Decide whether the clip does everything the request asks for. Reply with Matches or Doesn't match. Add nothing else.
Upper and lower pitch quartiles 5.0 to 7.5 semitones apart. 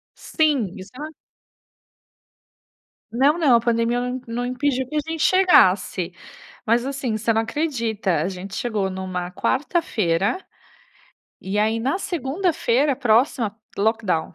Matches